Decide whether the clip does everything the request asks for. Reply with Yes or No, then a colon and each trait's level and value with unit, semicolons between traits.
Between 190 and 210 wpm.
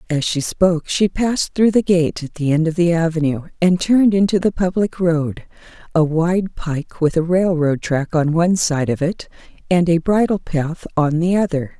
Yes: average, 200 wpm